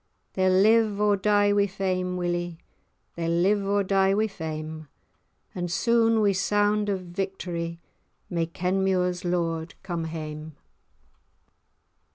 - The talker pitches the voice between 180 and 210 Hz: Yes, medium, 185 Hz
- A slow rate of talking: Yes, slow, 120 wpm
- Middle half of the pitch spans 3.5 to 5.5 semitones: No, average, 3.1 semitones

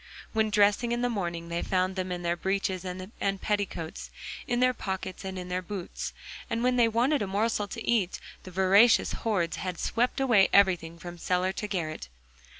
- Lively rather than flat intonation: No, average, 3.7 semitones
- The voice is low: No, high, 190 Hz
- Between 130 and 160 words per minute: No, average, 185 wpm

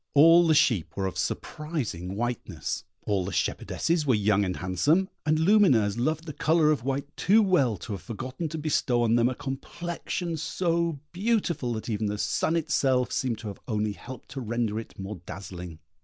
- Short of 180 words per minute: No, average, 185 wpm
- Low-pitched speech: Yes, low, 130 Hz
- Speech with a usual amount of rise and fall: No, wide, 7.3 semitones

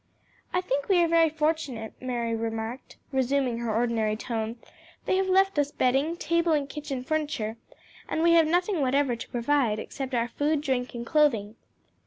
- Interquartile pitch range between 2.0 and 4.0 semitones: No, average, 5.0 semitones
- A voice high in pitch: Yes, very high, 275 Hz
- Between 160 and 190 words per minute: Yes, average, 170 wpm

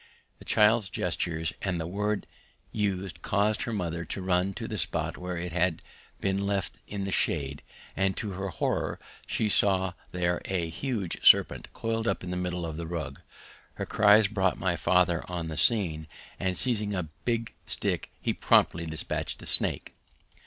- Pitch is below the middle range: Yes, very low, 95 Hz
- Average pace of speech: Yes, average, 175 wpm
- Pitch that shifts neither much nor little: Yes, average, 3.1 semitones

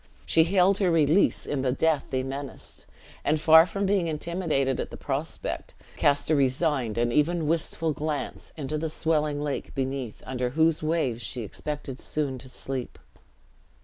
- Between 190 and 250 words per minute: No, average, 160 wpm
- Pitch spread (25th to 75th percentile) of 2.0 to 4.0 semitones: Yes, average, 3.4 semitones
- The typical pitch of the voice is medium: Yes, medium, 150 Hz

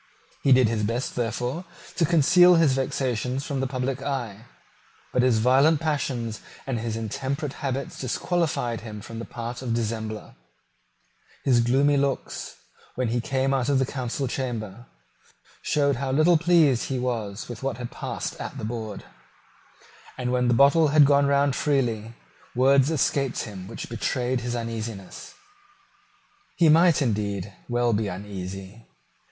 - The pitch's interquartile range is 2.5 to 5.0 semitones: Yes, average, 3.4 semitones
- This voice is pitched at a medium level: No, low, 125 Hz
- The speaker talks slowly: No, average, 150 wpm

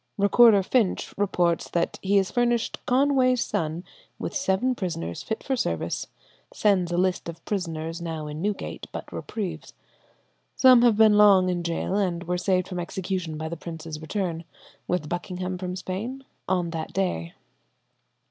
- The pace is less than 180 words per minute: Yes, average, 155 wpm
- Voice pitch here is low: No, medium, 185 Hz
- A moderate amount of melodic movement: Yes, average, 3.6 semitones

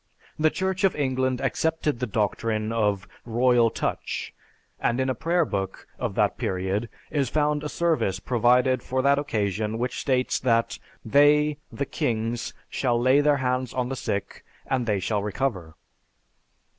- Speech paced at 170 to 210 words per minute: No, average, 155 wpm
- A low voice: Yes, low, 125 Hz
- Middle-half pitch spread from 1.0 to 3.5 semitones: No, average, 4.3 semitones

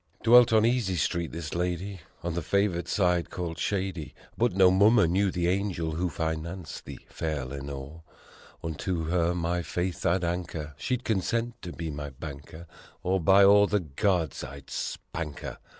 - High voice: No, very low, 85 Hz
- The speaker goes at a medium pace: Yes, average, 165 wpm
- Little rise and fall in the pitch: No, average, 3.3 semitones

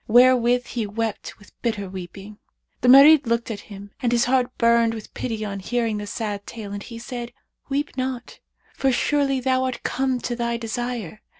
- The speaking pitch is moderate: No, high, 235 Hz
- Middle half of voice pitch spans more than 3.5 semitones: No, average, 3.0 semitones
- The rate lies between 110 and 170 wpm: No, average, 185 wpm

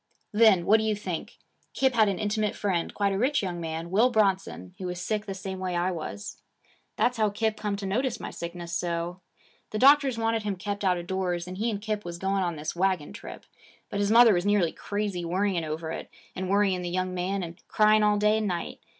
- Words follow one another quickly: Yes, fast, 225 wpm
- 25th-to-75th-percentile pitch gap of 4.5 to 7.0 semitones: No, average, 3.2 semitones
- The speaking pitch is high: Yes, high, 195 Hz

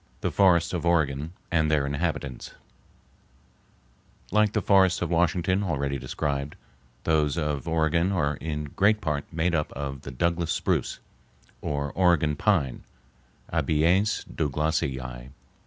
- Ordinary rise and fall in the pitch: Yes, average, 3.4 semitones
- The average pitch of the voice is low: Yes, very low, 80 Hz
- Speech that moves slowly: Yes, slow, 125 wpm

